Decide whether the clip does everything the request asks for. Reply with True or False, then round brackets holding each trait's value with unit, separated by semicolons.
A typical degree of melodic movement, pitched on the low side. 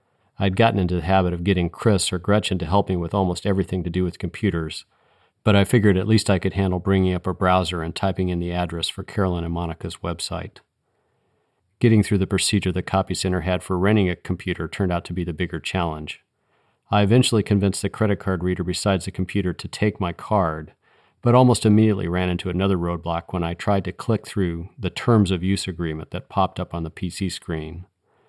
False (2.3 semitones; 95 Hz)